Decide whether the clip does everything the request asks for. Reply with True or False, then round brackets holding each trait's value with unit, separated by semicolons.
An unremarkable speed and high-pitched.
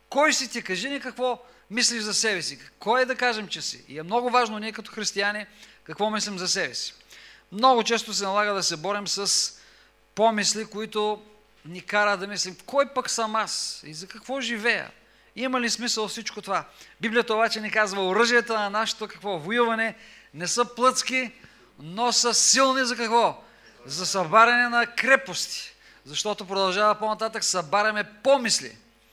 True (165 wpm; 220 Hz)